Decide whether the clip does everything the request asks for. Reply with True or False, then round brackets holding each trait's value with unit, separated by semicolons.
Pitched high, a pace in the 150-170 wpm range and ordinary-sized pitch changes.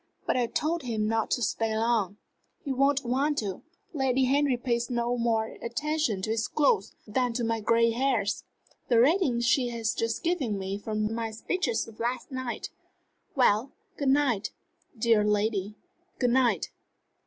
True (235 Hz; 160 wpm; 3.2 semitones)